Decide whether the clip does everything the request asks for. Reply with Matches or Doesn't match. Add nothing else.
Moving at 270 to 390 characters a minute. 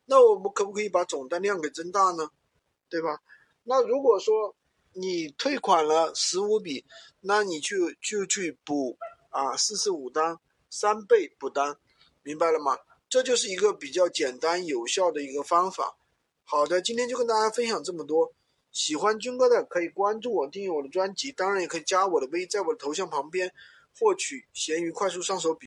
Matches